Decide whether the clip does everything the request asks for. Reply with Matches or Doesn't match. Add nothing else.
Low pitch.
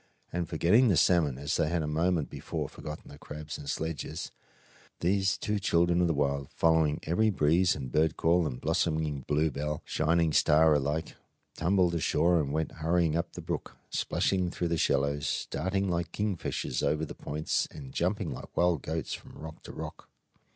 Matches